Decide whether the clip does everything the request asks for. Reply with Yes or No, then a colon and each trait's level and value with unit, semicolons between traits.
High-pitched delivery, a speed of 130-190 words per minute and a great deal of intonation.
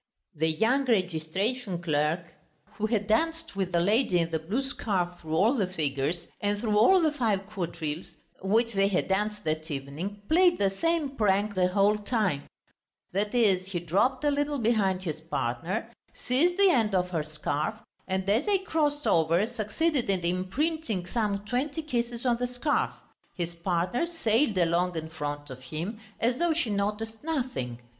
Yes: high, 205 Hz; average, 170 wpm; wide, 6.1 semitones